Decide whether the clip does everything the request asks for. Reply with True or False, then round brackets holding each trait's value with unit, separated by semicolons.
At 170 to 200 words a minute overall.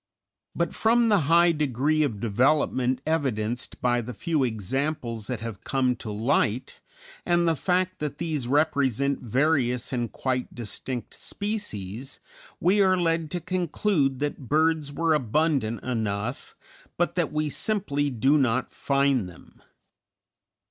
False (135 wpm)